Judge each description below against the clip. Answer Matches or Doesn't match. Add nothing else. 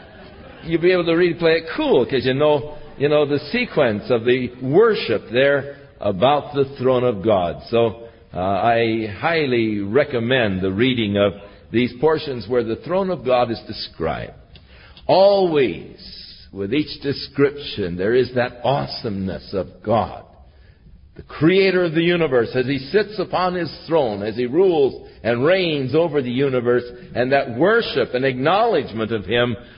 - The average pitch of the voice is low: Matches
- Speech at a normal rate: Matches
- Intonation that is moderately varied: Doesn't match